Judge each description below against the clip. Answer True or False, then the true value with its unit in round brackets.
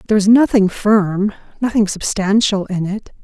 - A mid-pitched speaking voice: False (205 Hz)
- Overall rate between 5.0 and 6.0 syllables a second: False (4.8 syllables/s)